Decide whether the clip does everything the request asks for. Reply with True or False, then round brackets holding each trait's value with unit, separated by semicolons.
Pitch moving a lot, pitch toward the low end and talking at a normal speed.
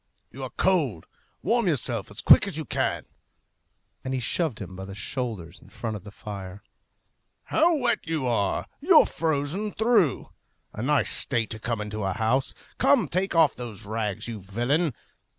True (7.7 semitones; 120 Hz; 170 wpm)